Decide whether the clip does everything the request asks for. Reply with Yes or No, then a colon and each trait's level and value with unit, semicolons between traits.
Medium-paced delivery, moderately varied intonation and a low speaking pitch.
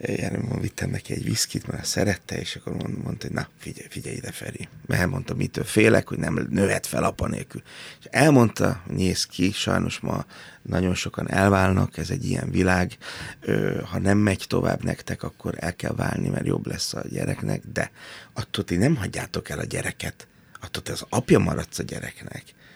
No: fast, 180 wpm; average, 3.7 semitones; very low, 95 Hz